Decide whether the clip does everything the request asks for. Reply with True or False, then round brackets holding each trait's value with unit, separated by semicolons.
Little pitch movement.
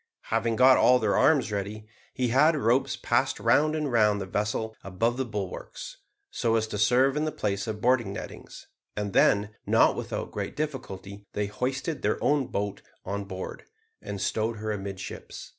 False (4.2 semitones)